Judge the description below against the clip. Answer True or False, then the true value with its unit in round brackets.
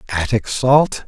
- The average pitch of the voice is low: True (125 Hz)